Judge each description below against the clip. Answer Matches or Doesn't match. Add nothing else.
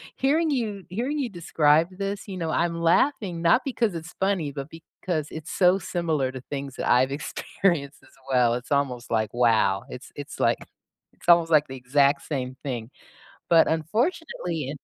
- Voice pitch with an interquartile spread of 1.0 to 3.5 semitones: Doesn't match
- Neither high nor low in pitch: Matches